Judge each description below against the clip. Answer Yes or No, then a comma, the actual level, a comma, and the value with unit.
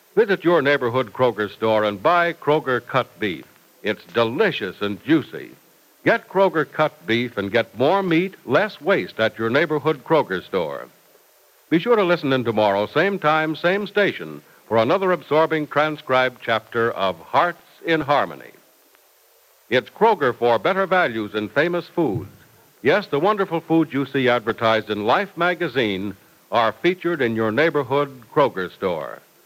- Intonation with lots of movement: Yes, wide, 7.0 semitones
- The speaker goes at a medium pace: Yes, average, 150 wpm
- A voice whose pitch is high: No, medium, 145 Hz